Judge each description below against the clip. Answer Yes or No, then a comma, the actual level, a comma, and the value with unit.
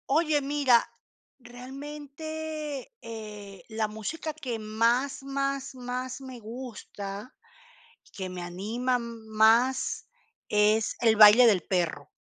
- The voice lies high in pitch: Yes, high, 240 Hz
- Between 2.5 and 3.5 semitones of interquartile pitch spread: No, average, 4.3 semitones